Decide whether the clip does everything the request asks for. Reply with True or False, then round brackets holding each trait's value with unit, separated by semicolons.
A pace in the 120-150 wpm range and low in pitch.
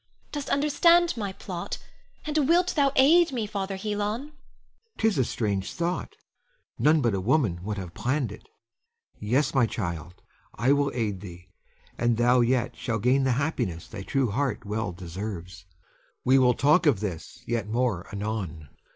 False (160 wpm; 125 Hz)